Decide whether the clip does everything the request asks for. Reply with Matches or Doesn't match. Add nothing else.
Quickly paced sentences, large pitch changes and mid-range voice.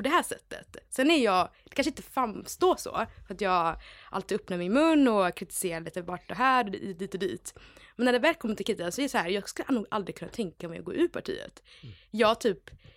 Doesn't match